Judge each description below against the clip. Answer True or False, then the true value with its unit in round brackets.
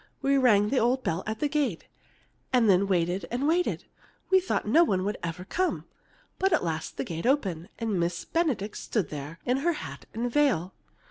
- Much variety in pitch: True (7.7 semitones)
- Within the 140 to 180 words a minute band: False (195 wpm)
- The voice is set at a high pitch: True (220 Hz)